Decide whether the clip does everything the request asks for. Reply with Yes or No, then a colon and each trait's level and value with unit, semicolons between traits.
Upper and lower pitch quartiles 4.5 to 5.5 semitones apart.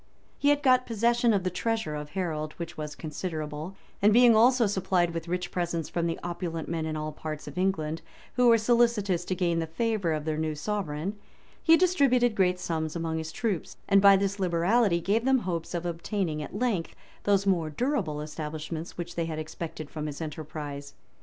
Yes: average, 5.0 semitones